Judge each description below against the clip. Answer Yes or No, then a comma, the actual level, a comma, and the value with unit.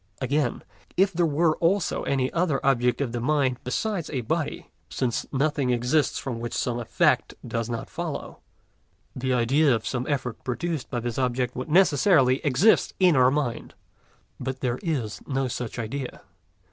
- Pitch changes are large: No, average, 3.6 semitones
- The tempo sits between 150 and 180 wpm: Yes, average, 160 wpm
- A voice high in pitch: No, low, 130 Hz